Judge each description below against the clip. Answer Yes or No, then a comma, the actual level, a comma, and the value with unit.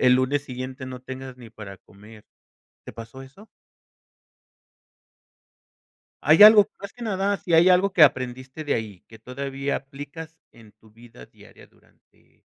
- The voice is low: Yes, low, 130 Hz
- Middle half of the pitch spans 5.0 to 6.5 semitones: Yes, wide, 5.5 semitones